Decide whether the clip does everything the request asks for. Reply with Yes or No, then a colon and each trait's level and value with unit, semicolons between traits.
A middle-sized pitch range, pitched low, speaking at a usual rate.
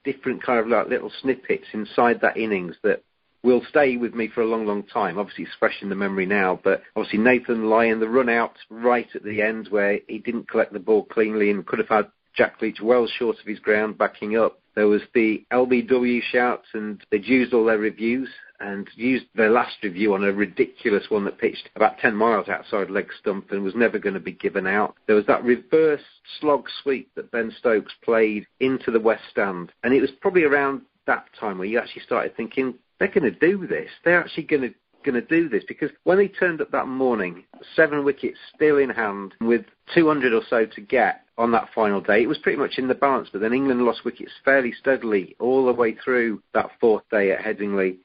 No: average, 3.7 semitones; low, 120 Hz; fast, 220 wpm